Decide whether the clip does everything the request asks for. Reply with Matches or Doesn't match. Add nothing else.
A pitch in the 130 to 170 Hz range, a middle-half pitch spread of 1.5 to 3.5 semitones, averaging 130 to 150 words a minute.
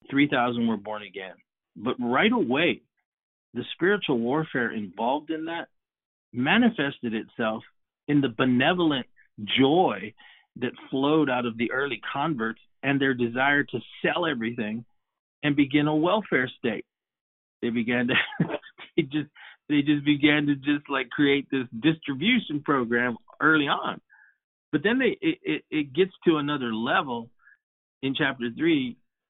Doesn't match